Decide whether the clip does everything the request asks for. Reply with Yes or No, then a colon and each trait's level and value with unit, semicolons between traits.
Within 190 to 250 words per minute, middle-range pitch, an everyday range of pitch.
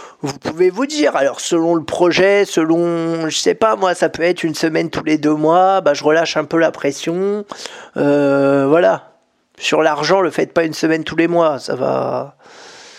Yes: average, 200 wpm; medium, 165 Hz; average, 3.5 semitones